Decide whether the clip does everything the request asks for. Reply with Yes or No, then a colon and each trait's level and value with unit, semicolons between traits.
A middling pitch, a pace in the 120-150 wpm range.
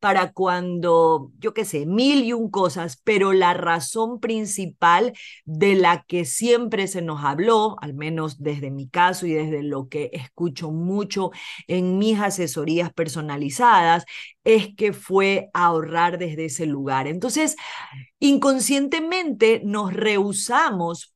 Yes: medium, 180 Hz; average, 130 wpm